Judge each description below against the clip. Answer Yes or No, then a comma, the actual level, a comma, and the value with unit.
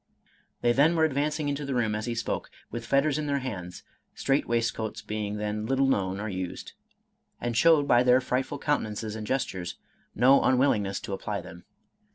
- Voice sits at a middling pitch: No, low, 120 Hz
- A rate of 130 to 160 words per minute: No, average, 180 wpm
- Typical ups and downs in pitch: Yes, average, 4.6 semitones